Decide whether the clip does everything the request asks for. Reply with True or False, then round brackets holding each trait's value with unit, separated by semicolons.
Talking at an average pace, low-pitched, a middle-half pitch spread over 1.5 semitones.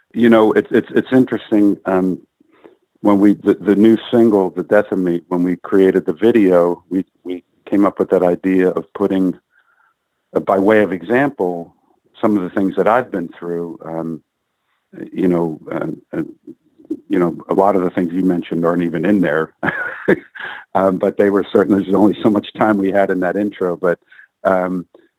True (190 wpm; 95 Hz; 2.6 semitones)